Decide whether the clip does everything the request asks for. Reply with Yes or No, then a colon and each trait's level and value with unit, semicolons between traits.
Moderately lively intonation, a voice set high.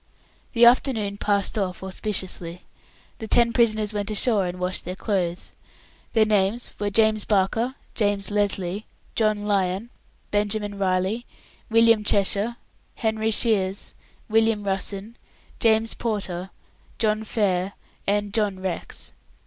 No: narrow, 2.3 semitones; high, 205 Hz